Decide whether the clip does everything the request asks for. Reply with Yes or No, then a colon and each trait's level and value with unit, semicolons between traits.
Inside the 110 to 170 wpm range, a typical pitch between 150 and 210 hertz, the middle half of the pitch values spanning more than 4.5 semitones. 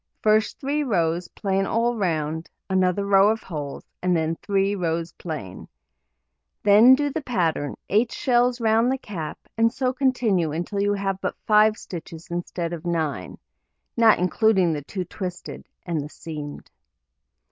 Yes: average, 150 wpm; high, 190 Hz; average, 5.1 semitones